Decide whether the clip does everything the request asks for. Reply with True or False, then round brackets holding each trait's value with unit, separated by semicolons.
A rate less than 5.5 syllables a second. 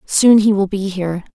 True (5.1 syllables/s)